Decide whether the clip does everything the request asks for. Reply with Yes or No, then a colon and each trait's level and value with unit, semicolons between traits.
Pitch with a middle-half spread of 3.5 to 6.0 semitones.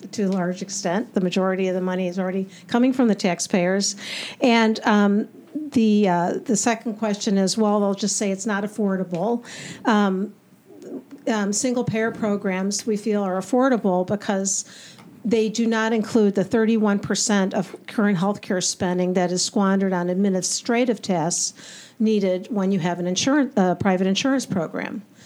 No: average, 2.9 semitones